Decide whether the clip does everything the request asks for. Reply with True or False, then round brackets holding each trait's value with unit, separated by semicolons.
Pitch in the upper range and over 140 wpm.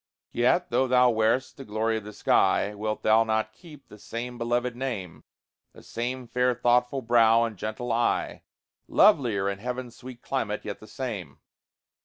False (120 Hz; 165 wpm)